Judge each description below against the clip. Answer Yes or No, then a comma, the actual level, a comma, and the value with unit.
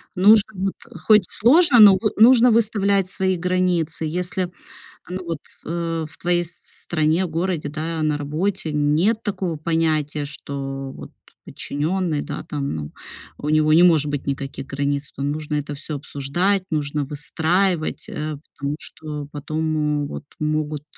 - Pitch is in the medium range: Yes, medium, 155 Hz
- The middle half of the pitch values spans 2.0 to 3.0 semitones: No, average, 3.9 semitones